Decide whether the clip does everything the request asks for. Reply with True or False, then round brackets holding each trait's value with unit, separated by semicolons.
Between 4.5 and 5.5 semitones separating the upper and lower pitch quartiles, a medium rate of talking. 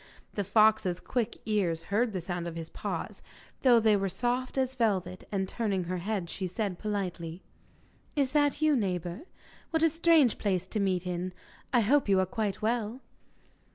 True (4.8 semitones; 175 wpm)